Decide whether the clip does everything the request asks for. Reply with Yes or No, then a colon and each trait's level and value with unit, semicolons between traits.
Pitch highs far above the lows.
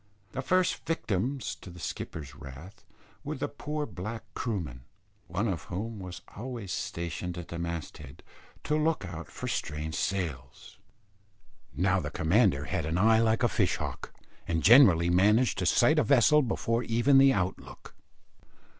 Yes: wide, 6.8 semitones